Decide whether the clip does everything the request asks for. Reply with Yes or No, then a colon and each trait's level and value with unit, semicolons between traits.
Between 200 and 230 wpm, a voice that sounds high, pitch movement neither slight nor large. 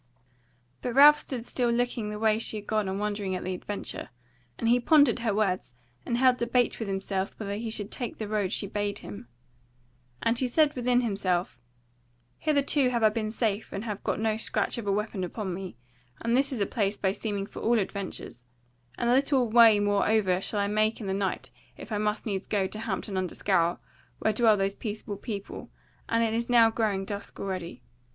Yes: fast, 205 wpm; high, 215 Hz; average, 3.0 semitones